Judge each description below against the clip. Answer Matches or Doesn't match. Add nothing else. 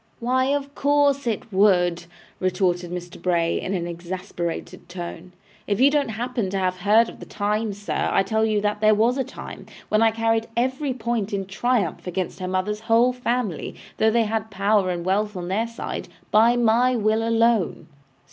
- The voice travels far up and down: Doesn't match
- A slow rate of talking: Doesn't match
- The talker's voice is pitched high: Matches